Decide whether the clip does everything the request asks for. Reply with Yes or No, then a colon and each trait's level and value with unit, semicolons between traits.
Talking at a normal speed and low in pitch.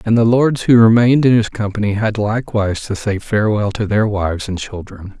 No: fast, 210 wpm; low, 105 Hz